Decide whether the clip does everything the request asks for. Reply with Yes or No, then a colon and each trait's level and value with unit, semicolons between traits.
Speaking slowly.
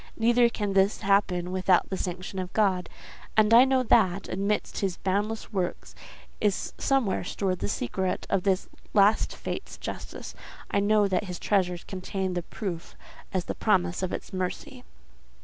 No: average, 160 wpm